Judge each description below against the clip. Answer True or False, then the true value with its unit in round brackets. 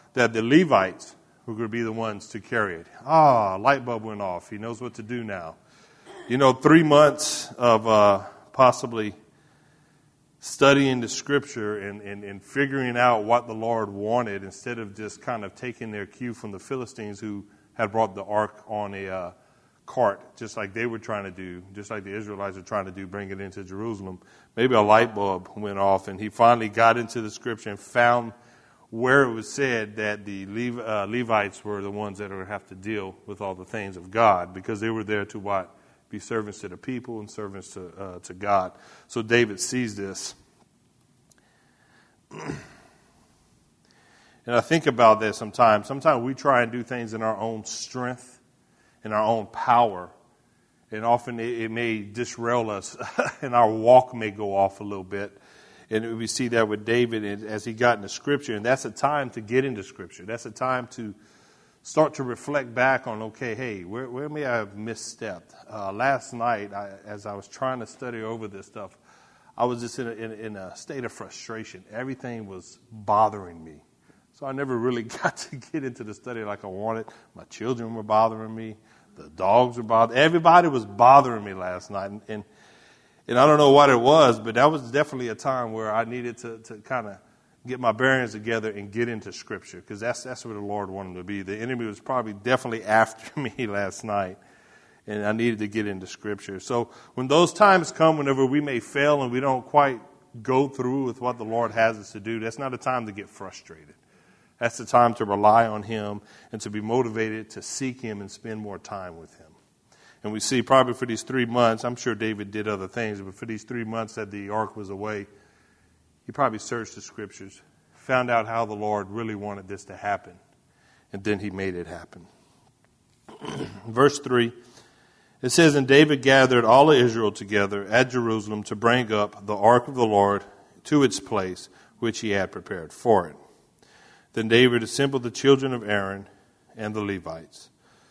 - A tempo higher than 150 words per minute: True (200 wpm)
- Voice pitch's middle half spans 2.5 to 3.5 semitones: True (3.1 semitones)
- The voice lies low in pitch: True (115 Hz)